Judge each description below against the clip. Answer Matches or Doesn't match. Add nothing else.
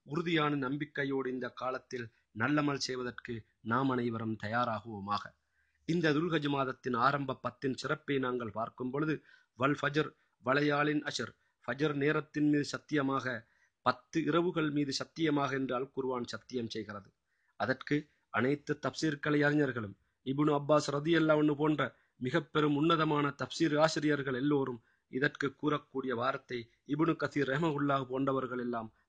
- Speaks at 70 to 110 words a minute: Doesn't match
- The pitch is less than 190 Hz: Matches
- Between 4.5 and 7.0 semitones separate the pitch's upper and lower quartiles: Doesn't match